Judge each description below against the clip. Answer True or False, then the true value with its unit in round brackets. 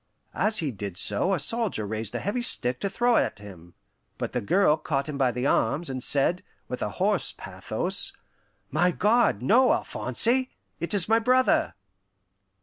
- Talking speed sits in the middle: True (170 wpm)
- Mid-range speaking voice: True (165 Hz)